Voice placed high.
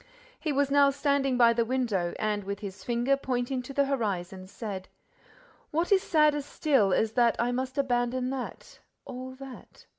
Yes: very high, 250 Hz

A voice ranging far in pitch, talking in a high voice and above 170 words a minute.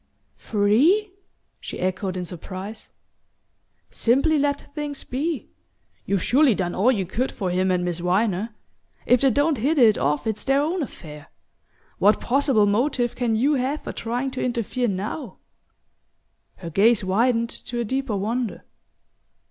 No: wide, 5.7 semitones; high, 230 Hz; average, 150 wpm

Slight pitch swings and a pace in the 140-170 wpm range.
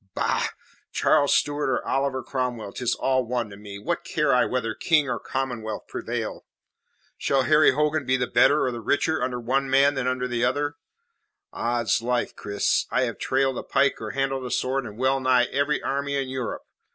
No: narrow, 2.2 semitones; average, 185 wpm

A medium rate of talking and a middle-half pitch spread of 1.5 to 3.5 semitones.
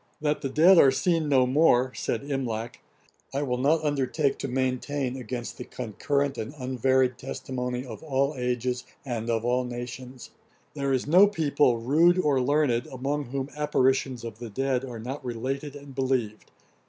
Yes: average, 165 wpm; narrow, 2.5 semitones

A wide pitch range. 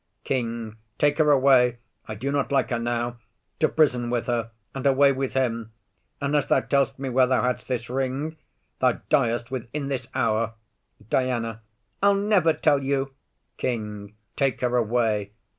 No: average, 3.0 semitones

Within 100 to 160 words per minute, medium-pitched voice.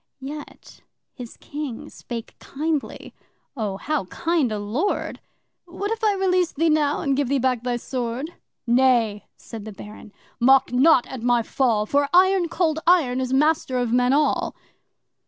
No: average, 155 wpm; very high, 265 Hz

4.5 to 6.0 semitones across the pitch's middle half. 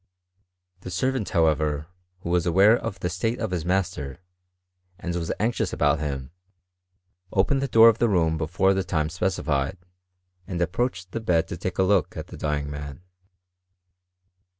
No: average, 3.8 semitones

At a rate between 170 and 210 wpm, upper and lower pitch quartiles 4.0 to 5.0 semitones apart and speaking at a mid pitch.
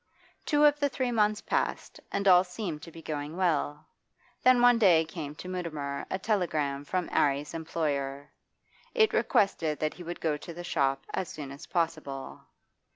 Yes: average, 175 wpm; average, 4.6 semitones; medium, 165 Hz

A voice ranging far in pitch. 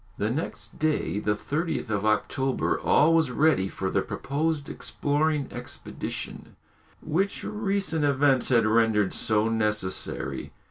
Yes: wide, 6.5 semitones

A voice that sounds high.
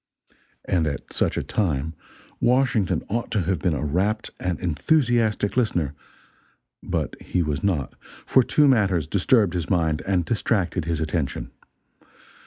No: very low, 90 Hz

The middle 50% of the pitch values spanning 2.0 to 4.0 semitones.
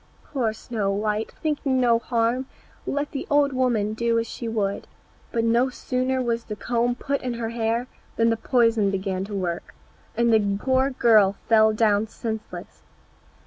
Yes: narrow, 2.6 semitones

